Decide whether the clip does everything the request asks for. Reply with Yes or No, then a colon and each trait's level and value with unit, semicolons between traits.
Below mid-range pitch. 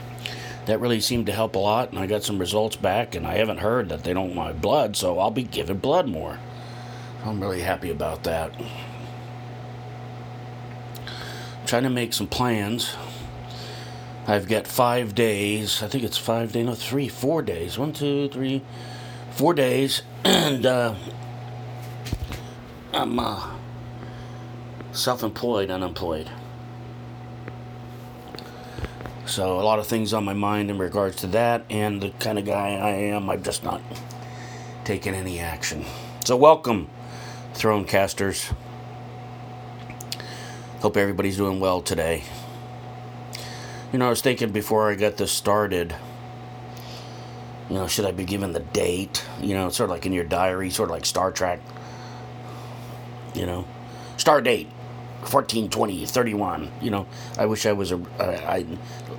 Yes: low, 120 Hz